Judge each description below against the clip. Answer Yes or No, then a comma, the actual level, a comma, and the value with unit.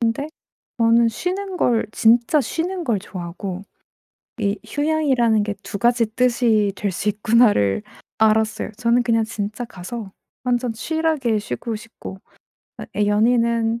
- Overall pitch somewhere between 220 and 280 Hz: Yes, high, 230 Hz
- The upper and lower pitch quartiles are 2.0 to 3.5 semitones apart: Yes, average, 2.7 semitones